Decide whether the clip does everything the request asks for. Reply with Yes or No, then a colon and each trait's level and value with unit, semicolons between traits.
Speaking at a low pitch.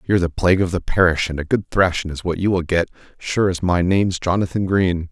Yes: very low, 90 Hz